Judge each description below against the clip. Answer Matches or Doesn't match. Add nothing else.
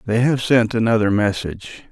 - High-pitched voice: Doesn't match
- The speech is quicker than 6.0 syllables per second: Doesn't match